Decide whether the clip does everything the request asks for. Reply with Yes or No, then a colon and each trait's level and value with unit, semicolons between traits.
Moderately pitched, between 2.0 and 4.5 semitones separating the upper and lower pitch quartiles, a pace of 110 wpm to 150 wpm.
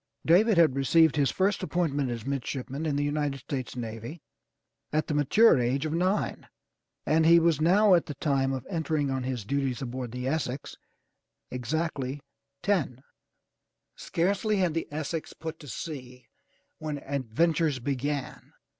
Yes: medium, 145 Hz; average, 3.9 semitones; average, 145 wpm